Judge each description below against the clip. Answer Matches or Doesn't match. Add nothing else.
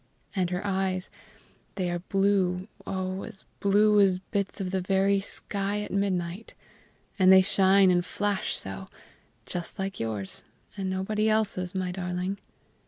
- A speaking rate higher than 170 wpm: Doesn't match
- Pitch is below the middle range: Doesn't match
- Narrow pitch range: Matches